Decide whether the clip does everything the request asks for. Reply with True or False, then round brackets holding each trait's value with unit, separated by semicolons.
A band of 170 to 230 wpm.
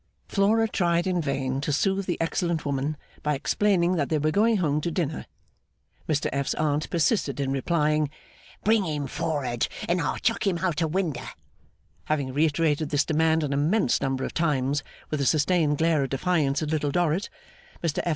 True (180 wpm)